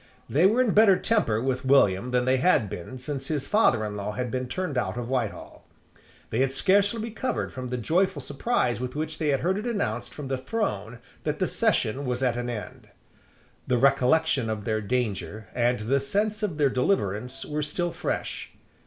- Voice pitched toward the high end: No, low, 130 Hz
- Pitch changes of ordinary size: No, wide, 6.2 semitones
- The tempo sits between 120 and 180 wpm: No, average, 195 wpm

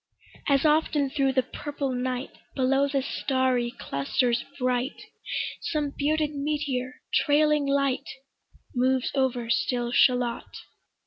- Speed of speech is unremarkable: No, slow, 110 wpm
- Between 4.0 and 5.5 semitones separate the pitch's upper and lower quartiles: No, narrow, 2.4 semitones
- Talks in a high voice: Yes, very high, 265 Hz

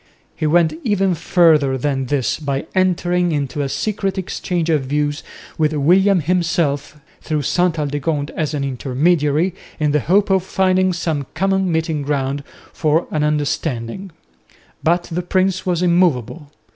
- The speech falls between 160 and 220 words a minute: No, average, 145 wpm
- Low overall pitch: No, medium, 160 Hz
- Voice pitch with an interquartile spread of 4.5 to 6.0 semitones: No, average, 3.8 semitones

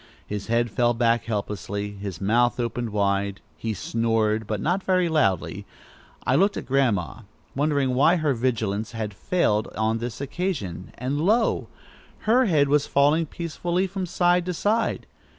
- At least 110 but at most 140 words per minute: No, average, 150 wpm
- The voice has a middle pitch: No, low, 120 Hz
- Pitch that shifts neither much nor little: No, wide, 7.6 semitones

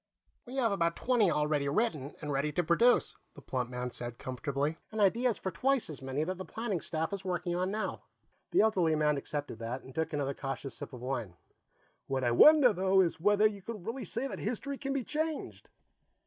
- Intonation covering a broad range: Yes, wide, 7.8 semitones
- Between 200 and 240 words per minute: Yes, fast, 205 wpm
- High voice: No, medium, 170 Hz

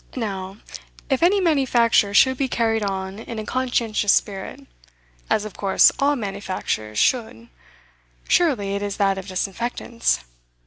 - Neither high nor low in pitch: No, high, 215 Hz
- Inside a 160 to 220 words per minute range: No, slow, 135 wpm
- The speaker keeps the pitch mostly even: No, average, 4.2 semitones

